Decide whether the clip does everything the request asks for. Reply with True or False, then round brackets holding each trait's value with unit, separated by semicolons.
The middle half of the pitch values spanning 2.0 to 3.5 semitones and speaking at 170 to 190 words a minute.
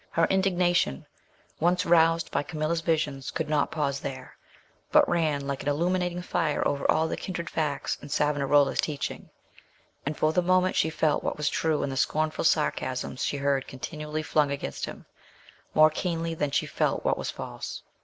True (2.8 semitones; 175 wpm)